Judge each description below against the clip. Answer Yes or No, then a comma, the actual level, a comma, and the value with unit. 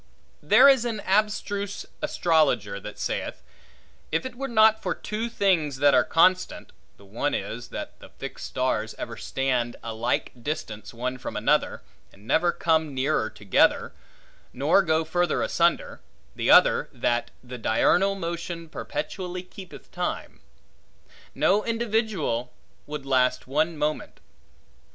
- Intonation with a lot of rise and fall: Yes, wide, 7.5 semitones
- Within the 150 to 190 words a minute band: No, slow, 135 wpm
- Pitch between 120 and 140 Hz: No, medium, 160 Hz